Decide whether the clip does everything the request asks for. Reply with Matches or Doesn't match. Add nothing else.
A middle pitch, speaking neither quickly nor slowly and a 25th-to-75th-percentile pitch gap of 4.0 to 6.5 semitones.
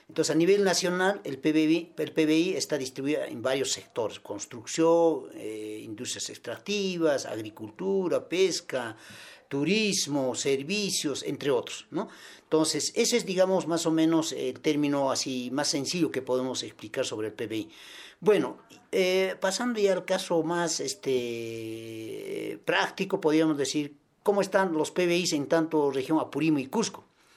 Matches